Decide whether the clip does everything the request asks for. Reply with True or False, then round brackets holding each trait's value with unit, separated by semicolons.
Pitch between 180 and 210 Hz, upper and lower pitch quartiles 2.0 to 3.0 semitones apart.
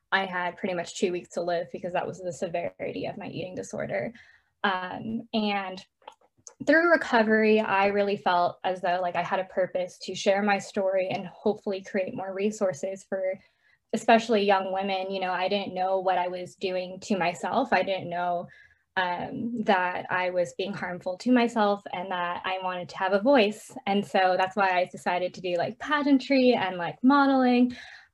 True (190 Hz; 2.6 semitones)